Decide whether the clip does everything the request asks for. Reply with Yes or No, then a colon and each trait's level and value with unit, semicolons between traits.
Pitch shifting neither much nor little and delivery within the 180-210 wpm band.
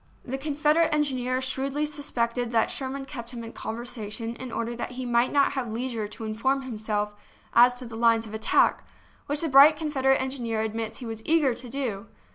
Yes: average, 3.1 semitones; average, 195 wpm